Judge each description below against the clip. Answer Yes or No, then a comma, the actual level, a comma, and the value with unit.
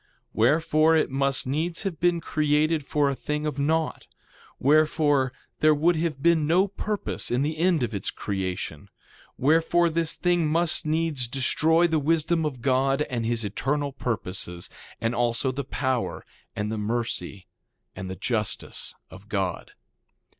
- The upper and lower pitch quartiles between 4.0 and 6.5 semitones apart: Yes, average, 5.1 semitones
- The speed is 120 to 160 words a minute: Yes, average, 155 wpm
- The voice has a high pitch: No, medium, 145 Hz